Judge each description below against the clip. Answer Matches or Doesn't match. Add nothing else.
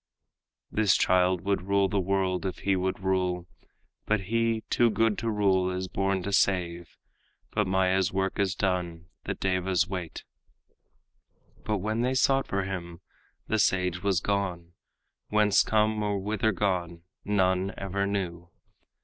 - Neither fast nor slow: Matches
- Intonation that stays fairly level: Matches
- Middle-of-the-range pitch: Doesn't match